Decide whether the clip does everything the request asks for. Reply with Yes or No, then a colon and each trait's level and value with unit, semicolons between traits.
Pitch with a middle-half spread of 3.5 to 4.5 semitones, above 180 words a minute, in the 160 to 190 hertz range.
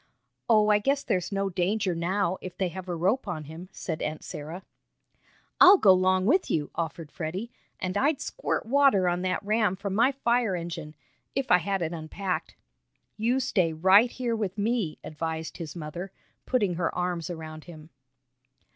No: average, 4.2 semitones; average, 175 wpm; medium, 185 Hz